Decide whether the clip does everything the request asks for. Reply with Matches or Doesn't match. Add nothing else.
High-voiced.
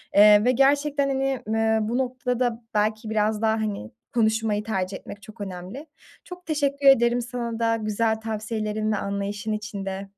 Matches